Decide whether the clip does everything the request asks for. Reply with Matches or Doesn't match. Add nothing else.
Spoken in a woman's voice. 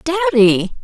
Matches